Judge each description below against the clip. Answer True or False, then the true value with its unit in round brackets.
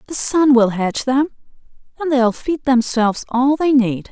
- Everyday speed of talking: True (190 wpm)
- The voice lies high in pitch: True (260 Hz)